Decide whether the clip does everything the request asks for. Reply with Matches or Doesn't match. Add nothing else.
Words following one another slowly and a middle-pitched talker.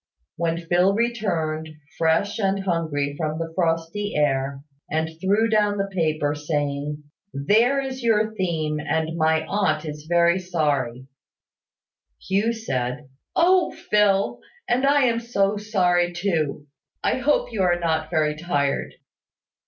Matches